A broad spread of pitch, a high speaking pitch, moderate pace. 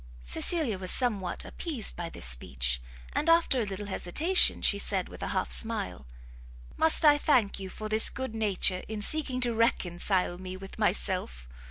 Yes: wide, 5.7 semitones; high, 210 Hz; average, 170 wpm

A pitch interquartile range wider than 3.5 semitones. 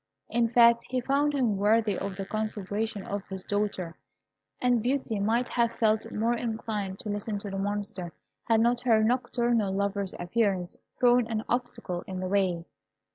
No: average, 3.0 semitones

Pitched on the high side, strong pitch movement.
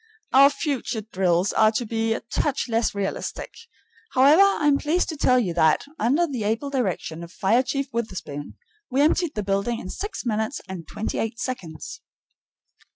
Yes: high, 230 Hz; wide, 6.0 semitones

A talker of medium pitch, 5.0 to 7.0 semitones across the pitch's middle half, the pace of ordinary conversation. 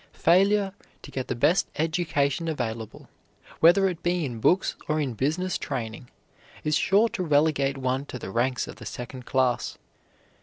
Yes: medium, 145 Hz; wide, 5.4 semitones; average, 160 wpm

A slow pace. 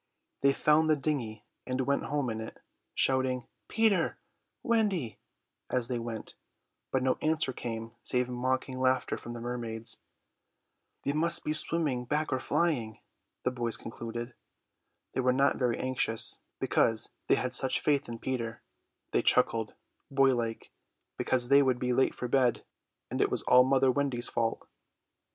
No: average, 150 wpm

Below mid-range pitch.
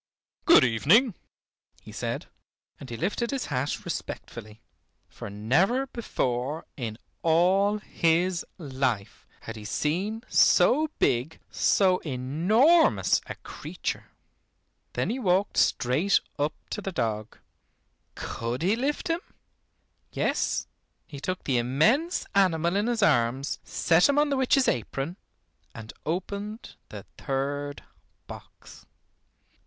No: medium, 165 Hz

